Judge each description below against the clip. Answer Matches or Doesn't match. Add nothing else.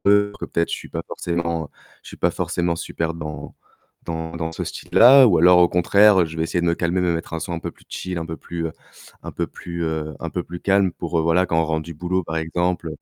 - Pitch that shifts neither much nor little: Doesn't match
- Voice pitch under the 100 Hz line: Matches